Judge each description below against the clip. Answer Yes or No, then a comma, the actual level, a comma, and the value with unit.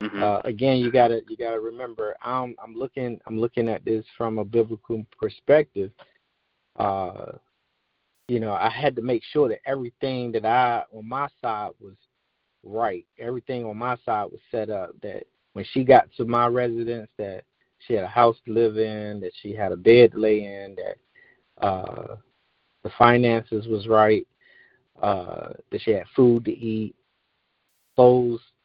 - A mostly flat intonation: Yes, narrow, 2.3 semitones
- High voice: No, low, 120 Hz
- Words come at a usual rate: Yes, average, 165 wpm